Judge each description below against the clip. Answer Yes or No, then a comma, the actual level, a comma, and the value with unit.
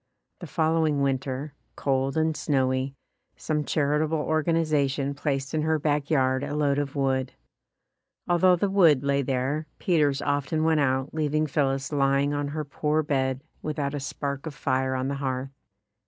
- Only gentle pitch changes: Yes, narrow, 2.3 semitones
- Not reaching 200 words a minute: Yes, average, 155 wpm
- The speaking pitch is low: No, medium, 145 Hz